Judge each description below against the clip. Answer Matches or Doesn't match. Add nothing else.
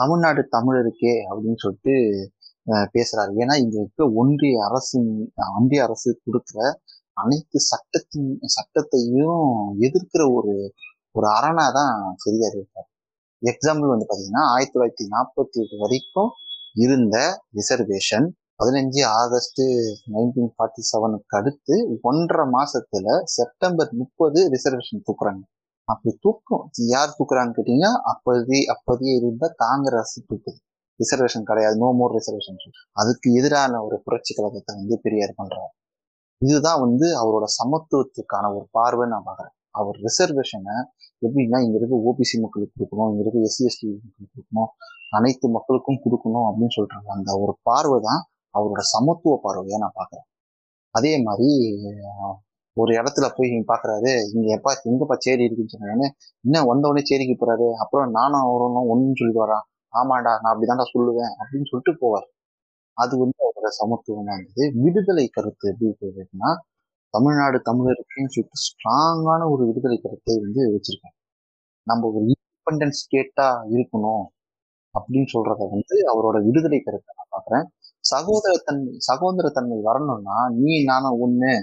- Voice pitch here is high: Doesn't match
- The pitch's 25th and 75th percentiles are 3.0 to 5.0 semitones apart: Matches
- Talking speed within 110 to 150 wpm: Matches